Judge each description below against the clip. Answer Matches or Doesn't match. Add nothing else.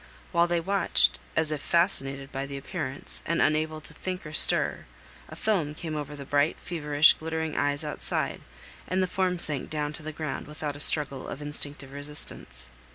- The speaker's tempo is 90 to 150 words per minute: Doesn't match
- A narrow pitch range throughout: Matches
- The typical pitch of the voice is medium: Matches